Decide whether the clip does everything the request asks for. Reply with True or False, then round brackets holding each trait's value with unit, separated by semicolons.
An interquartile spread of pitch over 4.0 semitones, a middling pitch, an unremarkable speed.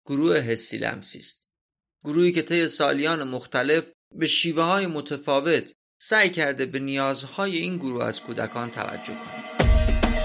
True (4.7 semitones; 145 Hz; 135 wpm)